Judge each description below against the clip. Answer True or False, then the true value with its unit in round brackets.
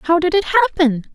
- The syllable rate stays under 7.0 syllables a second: False (7.3 syllables/s)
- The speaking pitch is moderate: False (300 Hz)